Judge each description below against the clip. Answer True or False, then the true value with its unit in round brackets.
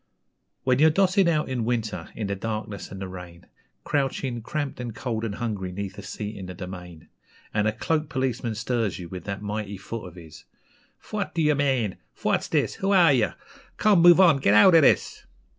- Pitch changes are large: True (6.4 semitones)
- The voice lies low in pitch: True (115 Hz)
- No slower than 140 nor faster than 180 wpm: False (195 wpm)